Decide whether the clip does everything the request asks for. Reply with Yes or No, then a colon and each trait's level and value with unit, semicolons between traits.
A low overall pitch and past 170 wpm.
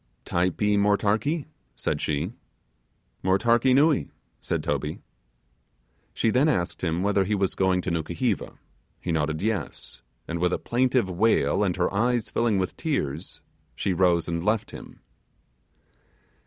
No: low, 100 Hz; slow, 135 wpm